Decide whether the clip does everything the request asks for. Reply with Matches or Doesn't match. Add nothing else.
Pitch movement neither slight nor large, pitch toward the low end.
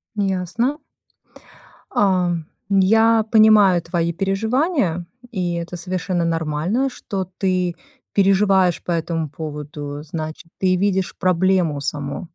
Doesn't match